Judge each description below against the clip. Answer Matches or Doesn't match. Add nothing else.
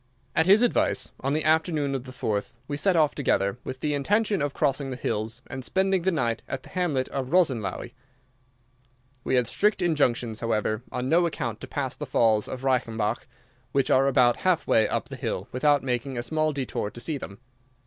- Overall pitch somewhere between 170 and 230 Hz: Doesn't match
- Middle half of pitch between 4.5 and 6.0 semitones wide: Matches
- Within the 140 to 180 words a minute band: Doesn't match